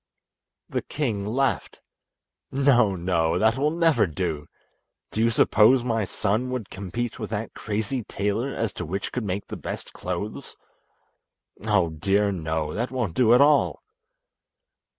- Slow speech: No, average, 145 wpm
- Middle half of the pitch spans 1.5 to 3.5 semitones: No, average, 4.7 semitones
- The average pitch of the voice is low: Yes, low, 110 Hz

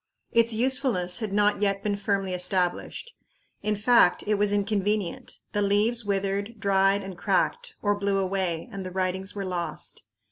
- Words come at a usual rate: Yes, average, 155 wpm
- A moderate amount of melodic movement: No, narrow, 1.8 semitones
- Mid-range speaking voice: No, high, 200 Hz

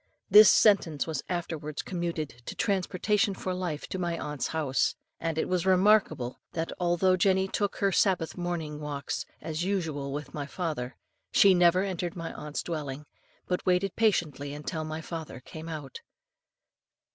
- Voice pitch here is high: No, medium, 170 Hz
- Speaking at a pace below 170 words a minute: Yes, average, 155 wpm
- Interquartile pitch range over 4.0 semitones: No, average, 3.6 semitones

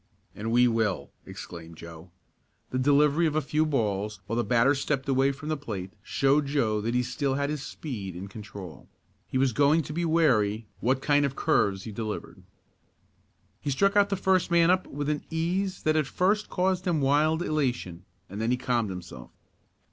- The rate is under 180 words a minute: No, average, 190 wpm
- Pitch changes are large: Yes, wide, 6.2 semitones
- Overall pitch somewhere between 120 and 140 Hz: Yes, low, 135 Hz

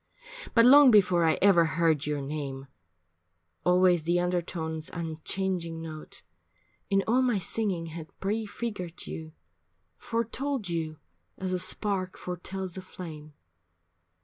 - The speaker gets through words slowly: Yes, slow, 120 wpm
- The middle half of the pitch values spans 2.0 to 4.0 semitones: Yes, average, 3.5 semitones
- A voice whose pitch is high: No, medium, 180 Hz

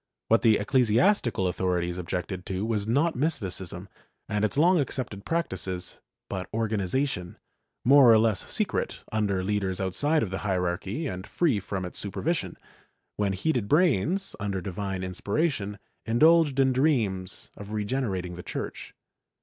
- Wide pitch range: Yes, wide, 6.1 semitones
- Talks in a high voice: No, low, 105 Hz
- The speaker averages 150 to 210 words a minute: No, average, 140 wpm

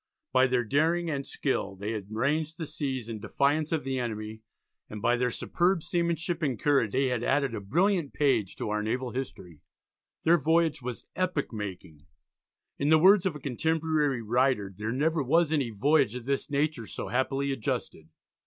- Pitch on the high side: No, low, 135 Hz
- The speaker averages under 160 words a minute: No, average, 180 wpm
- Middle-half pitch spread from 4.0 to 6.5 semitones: Yes, wide, 5.6 semitones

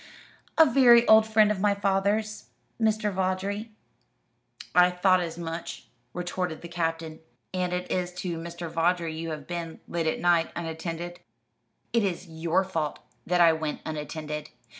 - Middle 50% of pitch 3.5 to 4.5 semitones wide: No, average, 2.9 semitones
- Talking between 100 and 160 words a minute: Yes, average, 150 wpm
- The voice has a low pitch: No, medium, 175 Hz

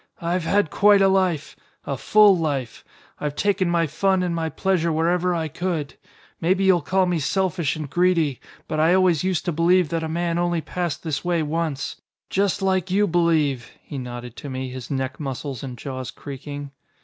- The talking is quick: No, average, 185 wpm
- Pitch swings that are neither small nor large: Yes, average, 4.2 semitones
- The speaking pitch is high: No, medium, 165 Hz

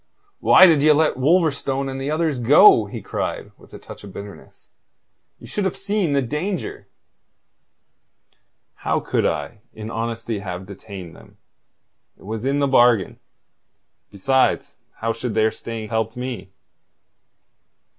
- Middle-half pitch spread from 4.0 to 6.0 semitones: Yes, average, 5.1 semitones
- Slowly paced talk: No, average, 145 wpm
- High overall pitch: No, low, 120 Hz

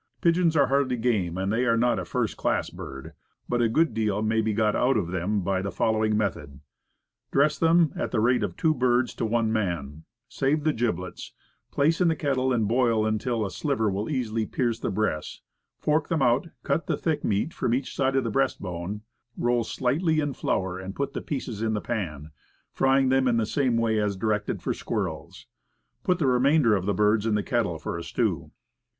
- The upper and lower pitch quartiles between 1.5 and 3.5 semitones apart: No, average, 4.5 semitones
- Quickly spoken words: Yes, fast, 210 wpm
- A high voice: No, low, 115 Hz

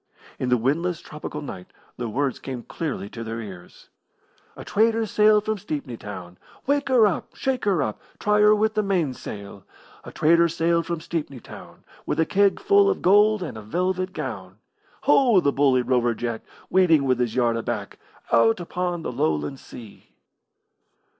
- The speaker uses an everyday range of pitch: No, wide, 9.0 semitones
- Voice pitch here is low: No, medium, 155 Hz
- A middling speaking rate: Yes, average, 170 wpm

